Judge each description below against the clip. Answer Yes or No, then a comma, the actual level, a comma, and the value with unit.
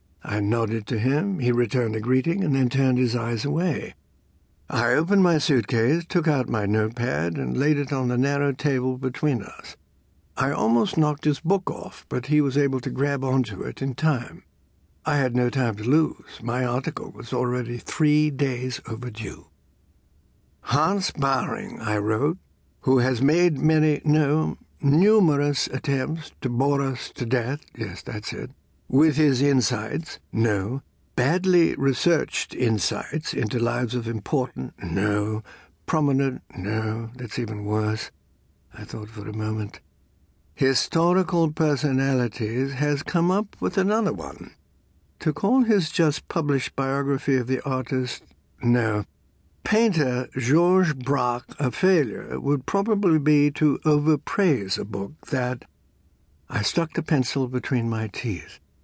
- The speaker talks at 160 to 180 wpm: No, average, 140 wpm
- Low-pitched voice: Yes, low, 130 Hz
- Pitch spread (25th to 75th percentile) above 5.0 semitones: Yes, wide, 5.4 semitones